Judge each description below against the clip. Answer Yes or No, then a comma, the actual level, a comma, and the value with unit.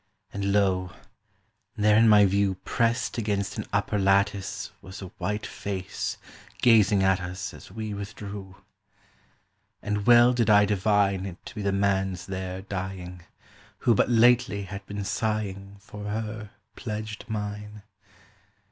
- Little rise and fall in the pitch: Yes, narrow, 1.8 semitones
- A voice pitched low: Yes, low, 100 Hz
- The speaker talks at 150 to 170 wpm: No, average, 140 wpm